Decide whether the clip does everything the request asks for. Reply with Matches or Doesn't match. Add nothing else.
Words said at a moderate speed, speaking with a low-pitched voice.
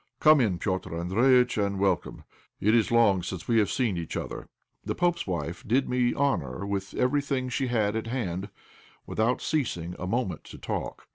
Matches